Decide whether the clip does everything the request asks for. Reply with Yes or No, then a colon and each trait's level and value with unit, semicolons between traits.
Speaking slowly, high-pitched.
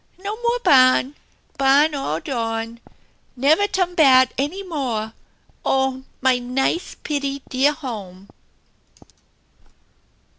Yes: slow, 100 wpm; very high, 270 Hz